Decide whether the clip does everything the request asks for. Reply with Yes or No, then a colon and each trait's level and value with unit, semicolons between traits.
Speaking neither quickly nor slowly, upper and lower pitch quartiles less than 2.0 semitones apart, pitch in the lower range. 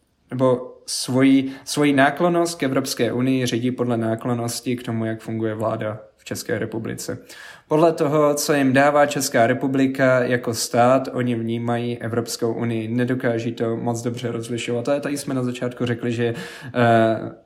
No: average, 150 wpm; narrow, 2.5 semitones; low, 125 Hz